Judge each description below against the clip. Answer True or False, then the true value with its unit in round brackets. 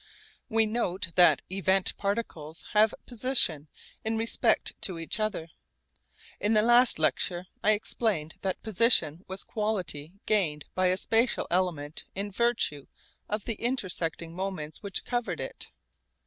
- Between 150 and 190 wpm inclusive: False (135 wpm)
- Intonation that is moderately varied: True (4.8 semitones)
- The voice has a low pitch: False (195 Hz)